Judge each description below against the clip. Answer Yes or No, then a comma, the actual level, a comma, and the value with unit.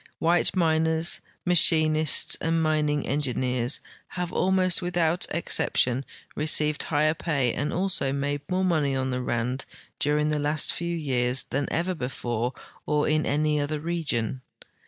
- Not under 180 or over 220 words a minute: No, average, 140 wpm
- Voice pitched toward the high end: No, medium, 150 Hz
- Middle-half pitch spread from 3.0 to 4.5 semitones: Yes, average, 3.3 semitones